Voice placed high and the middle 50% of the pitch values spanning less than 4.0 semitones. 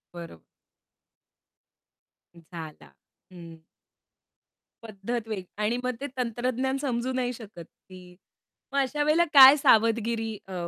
No: high, 230 Hz; wide, 5.6 semitones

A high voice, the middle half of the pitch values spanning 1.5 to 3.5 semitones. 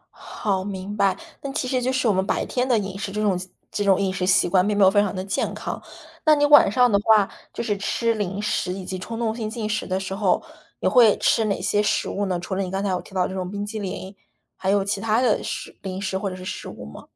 Yes: high, 200 Hz; narrow, 2.5 semitones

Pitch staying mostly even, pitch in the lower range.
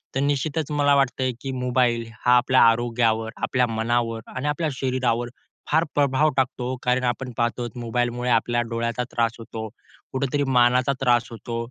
Yes: narrow, 2.1 semitones; low, 125 Hz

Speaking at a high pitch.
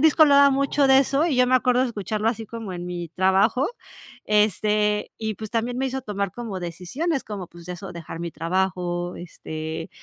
Yes: high, 210 Hz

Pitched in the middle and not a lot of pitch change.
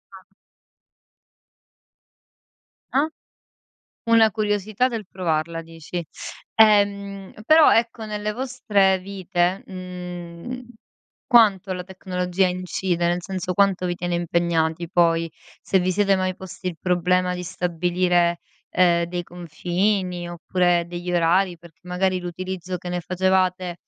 Yes: medium, 180 Hz; narrow, 2.0 semitones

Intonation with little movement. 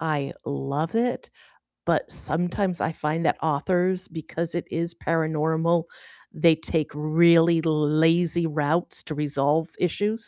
Yes: narrow, 1.8 semitones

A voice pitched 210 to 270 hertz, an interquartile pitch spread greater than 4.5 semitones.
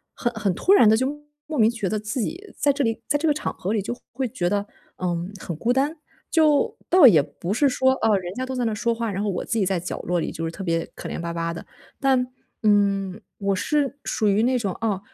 Yes: high, 220 Hz; wide, 5.6 semitones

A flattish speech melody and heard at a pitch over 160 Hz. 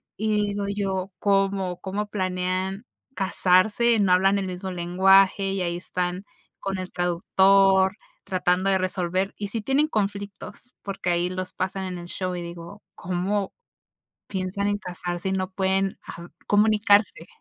Yes: narrow, 1.7 semitones; high, 190 Hz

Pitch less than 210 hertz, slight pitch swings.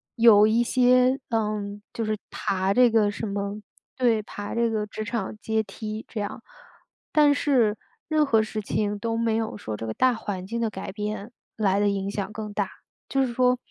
No: high, 215 Hz; narrow, 2.3 semitones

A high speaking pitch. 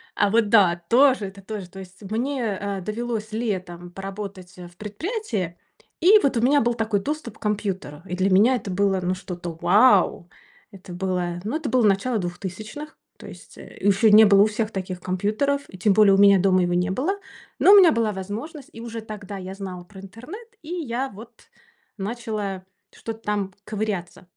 Yes: high, 205 Hz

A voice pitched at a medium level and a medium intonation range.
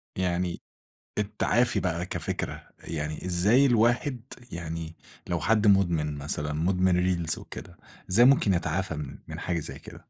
No: very low, 90 Hz; average, 4.0 semitones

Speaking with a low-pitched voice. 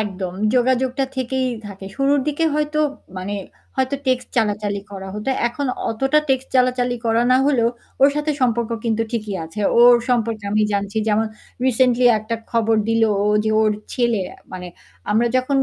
No: high, 235 Hz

